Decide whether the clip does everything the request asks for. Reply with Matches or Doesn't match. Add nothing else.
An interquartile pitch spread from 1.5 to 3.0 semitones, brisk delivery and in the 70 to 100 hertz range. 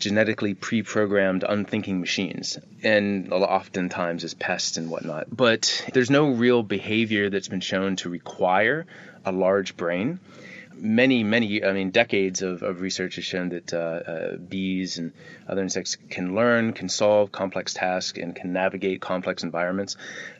Doesn't match